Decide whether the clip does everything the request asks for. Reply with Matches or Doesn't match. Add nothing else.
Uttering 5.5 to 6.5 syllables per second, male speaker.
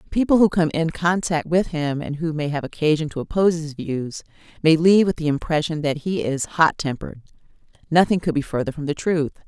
Doesn't match